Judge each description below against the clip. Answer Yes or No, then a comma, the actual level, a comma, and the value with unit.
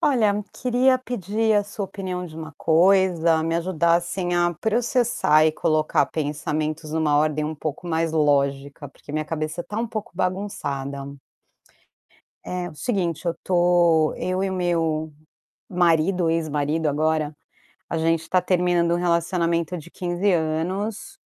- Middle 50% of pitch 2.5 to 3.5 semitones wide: Yes, average, 3.0 semitones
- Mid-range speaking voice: Yes, medium, 170 Hz